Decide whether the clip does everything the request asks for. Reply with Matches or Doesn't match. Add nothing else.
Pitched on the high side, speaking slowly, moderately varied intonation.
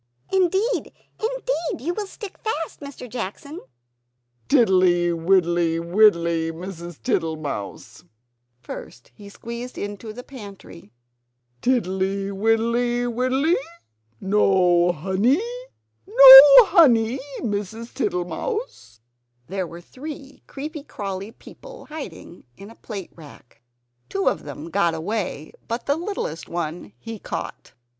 Doesn't match